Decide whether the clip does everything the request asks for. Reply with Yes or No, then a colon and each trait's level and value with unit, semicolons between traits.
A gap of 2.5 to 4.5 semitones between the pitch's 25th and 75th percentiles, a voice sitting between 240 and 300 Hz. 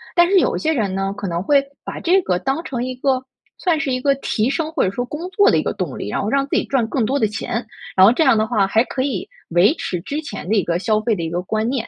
No: wide, 5.6 semitones; high, 245 Hz